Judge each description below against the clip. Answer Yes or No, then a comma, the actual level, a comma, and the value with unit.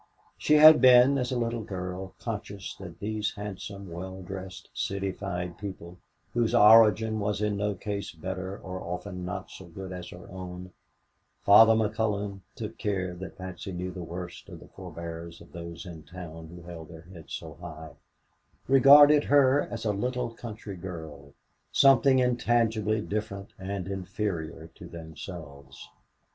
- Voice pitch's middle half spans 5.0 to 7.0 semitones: No, average, 3.8 semitones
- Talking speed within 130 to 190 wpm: Yes, average, 150 wpm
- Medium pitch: No, very low, 95 Hz